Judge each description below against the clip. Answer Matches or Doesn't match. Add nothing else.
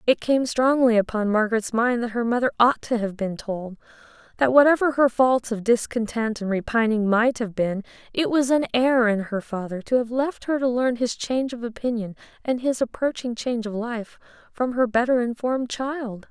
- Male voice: Doesn't match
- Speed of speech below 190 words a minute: Doesn't match